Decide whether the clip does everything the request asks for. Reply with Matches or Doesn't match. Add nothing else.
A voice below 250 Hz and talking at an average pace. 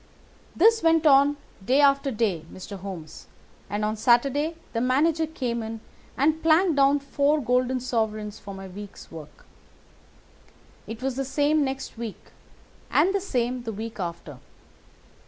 Doesn't match